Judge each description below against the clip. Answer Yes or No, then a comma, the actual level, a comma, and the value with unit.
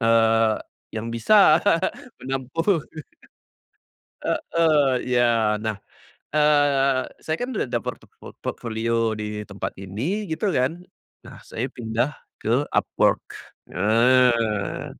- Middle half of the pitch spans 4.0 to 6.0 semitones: Yes, average, 4.9 semitones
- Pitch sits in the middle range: No, low, 120 Hz